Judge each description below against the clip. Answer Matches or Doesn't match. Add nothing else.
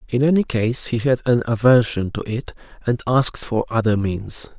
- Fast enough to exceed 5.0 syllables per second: Doesn't match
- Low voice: Matches